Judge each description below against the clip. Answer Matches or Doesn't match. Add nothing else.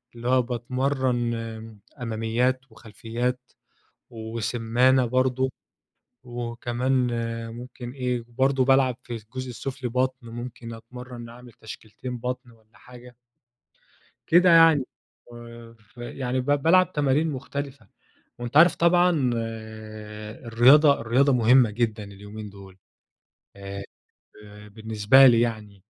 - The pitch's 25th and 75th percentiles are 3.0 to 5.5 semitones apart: Doesn't match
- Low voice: Matches